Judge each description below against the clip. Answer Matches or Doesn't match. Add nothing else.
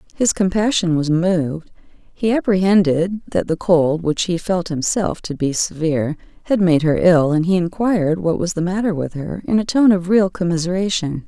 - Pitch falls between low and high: Matches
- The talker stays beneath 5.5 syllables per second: Matches